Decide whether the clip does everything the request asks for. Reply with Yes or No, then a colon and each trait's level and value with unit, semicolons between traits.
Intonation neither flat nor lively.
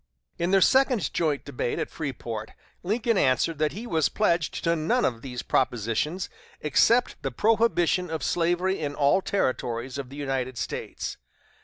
No: wide, 6.3 semitones